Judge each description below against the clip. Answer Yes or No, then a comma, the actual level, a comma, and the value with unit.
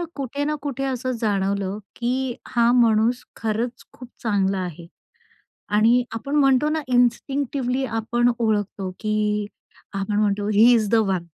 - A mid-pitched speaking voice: No, high, 230 Hz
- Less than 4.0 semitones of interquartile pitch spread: Yes, average, 3.4 semitones